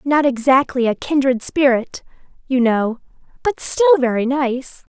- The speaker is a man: No, female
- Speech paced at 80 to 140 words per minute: Yes, slow, 135 wpm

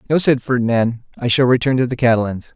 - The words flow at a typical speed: No, fast, 210 wpm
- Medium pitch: No, low, 125 Hz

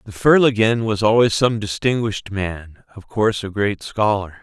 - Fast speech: No, average, 165 wpm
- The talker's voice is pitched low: Yes, low, 105 Hz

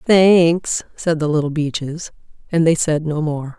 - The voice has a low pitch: No, medium, 160 Hz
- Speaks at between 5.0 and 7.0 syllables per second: No, 4.0 syllables/s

